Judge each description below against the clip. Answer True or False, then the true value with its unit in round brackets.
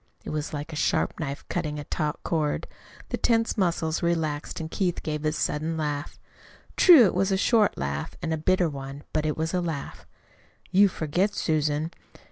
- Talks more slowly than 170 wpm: False (185 wpm)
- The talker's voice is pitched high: False (160 Hz)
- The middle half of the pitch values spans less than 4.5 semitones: True (3.2 semitones)